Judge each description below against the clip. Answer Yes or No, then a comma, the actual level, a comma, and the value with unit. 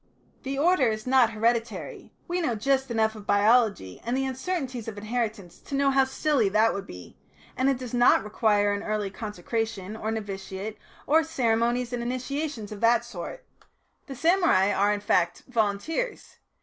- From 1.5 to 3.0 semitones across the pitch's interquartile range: No, average, 4.2 semitones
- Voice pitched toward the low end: No, high, 230 Hz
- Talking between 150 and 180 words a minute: Yes, average, 165 wpm